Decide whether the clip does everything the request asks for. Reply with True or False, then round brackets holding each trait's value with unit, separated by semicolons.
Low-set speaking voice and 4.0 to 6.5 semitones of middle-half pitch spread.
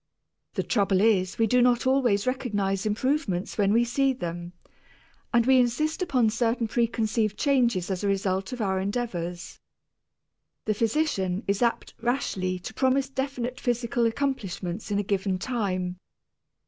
False (225 Hz; 4.5 semitones)